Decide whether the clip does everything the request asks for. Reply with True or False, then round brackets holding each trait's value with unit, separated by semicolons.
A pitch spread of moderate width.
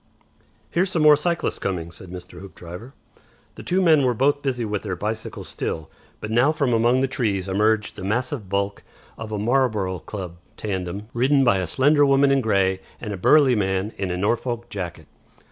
False (5.7 semitones)